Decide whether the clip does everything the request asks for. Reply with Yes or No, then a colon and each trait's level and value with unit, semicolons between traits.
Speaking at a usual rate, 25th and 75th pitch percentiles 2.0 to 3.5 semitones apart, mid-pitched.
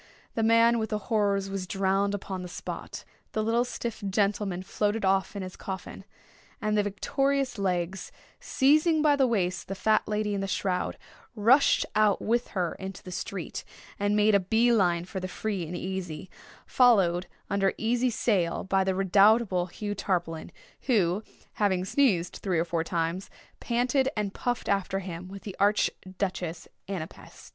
No: average, 165 wpm; average, 3.1 semitones; high, 195 Hz